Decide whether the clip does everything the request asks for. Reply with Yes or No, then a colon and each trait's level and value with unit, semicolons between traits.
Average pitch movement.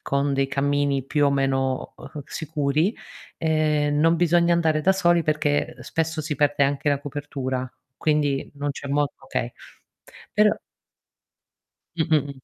No: narrow, 2.2 semitones